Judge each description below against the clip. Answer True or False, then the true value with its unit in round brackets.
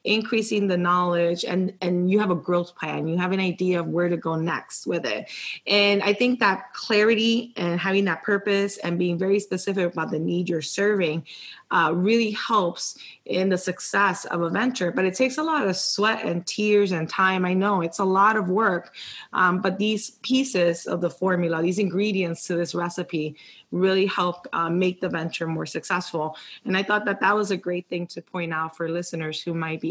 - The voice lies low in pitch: False (185 Hz)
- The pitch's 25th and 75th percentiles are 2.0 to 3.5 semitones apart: True (2.8 semitones)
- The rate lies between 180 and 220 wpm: True (205 wpm)